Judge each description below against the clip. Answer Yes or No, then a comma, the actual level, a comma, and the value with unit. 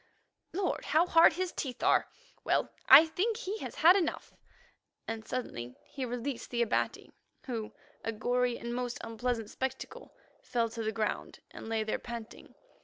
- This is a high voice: Yes, high, 245 Hz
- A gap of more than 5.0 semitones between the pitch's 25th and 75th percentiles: Yes, wide, 5.6 semitones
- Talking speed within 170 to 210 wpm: No, average, 160 wpm